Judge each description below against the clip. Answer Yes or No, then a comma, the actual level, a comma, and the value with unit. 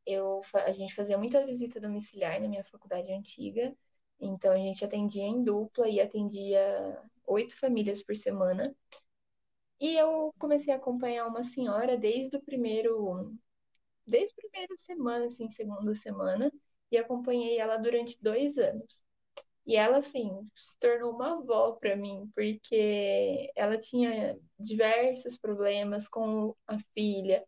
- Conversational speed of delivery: Yes, average, 140 wpm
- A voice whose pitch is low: No, high, 225 Hz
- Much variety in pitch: No, average, 3.7 semitones